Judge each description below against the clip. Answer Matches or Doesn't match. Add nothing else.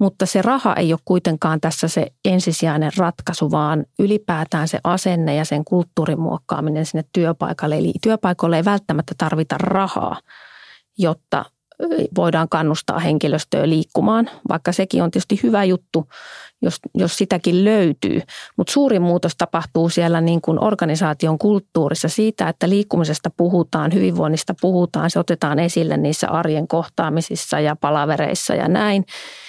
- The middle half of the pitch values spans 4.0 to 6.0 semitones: Doesn't match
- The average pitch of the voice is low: Doesn't match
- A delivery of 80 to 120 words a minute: Doesn't match